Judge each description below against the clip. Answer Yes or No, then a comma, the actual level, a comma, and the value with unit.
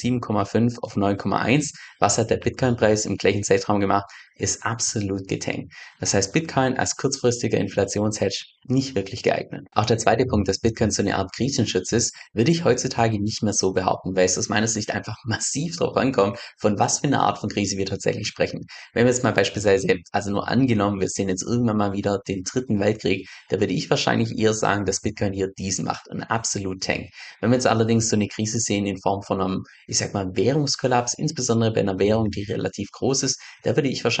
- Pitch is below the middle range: Yes, low, 105 Hz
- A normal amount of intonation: Yes, average, 3.2 semitones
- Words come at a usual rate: No, fast, 210 wpm